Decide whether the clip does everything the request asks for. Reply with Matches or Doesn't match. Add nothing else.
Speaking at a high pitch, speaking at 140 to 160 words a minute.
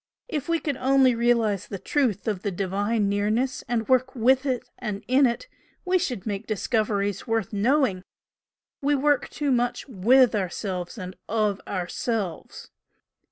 Matches